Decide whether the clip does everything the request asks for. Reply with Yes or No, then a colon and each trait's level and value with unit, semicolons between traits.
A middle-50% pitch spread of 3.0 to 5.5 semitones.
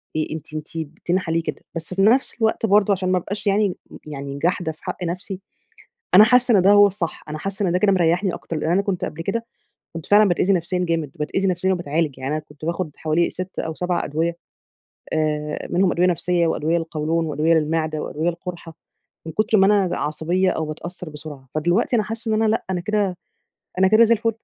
Yes: average, 3.7 semitones